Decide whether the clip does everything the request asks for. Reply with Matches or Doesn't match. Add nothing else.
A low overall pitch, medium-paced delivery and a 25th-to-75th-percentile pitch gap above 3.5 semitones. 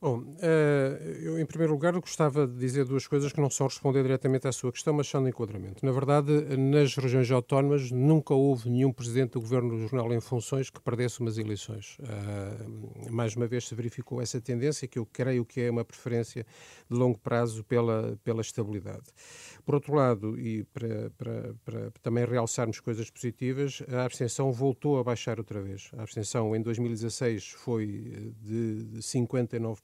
Doesn't match